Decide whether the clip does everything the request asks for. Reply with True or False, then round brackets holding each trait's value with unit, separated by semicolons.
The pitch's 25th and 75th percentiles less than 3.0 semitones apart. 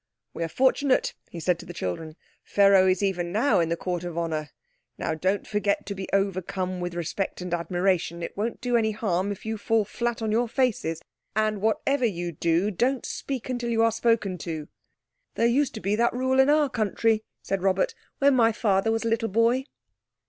False (4.6 semitones)